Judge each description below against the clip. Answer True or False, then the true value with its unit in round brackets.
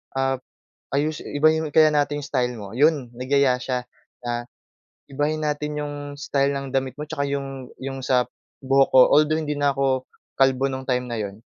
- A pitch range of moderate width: False (2.2 semitones)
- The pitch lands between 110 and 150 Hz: True (135 Hz)